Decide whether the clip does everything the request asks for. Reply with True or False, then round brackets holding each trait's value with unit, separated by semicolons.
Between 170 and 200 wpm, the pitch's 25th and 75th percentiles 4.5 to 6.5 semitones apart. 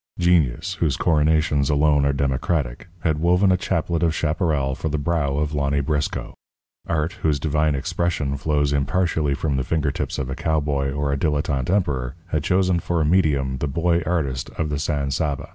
False (180 wpm; 2.8 semitones)